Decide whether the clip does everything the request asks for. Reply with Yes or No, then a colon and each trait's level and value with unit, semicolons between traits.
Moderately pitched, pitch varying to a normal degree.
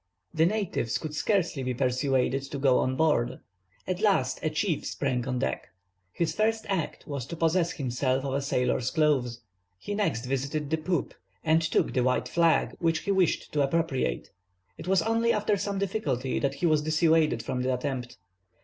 Yes: medium, 150 Hz; average, 4.8 semitones